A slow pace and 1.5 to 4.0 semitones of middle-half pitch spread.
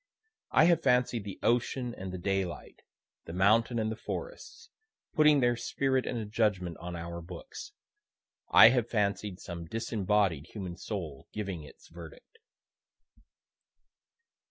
No: slow, 130 wpm; average, 5.2 semitones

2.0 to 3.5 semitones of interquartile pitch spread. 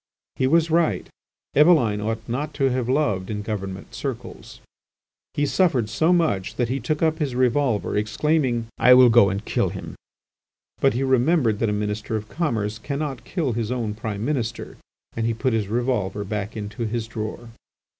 No: average, 4.6 semitones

